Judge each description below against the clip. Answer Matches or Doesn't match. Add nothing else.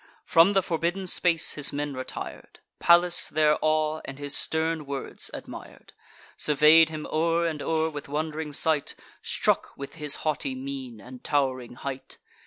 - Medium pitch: Matches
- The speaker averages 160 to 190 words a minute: Doesn't match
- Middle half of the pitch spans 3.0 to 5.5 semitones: Doesn't match